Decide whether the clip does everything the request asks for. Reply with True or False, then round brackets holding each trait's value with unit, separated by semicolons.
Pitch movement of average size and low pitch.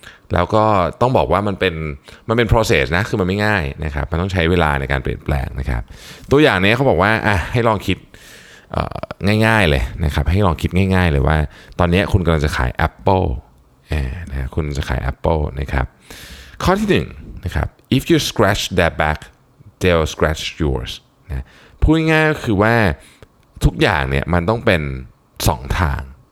False (6.4 semitones; 90 Hz)